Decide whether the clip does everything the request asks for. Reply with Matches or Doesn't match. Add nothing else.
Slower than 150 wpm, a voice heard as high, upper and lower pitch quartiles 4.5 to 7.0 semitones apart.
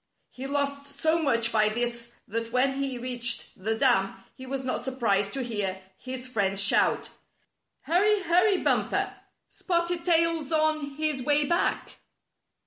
Matches